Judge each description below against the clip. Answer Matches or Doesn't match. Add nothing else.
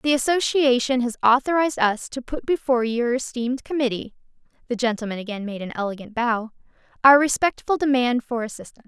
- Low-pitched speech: Doesn't match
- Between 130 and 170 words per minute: Matches